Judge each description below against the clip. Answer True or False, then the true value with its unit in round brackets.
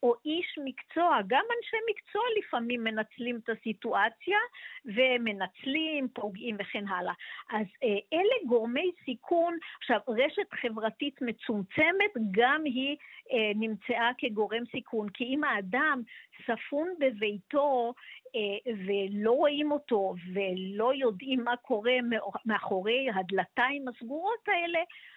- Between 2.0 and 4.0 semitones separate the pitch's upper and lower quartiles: False (5.3 semitones)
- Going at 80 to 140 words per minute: True (105 wpm)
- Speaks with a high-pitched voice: True (245 Hz)